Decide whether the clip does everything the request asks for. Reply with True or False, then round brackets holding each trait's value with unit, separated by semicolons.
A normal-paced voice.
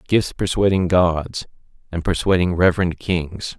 False (115 wpm)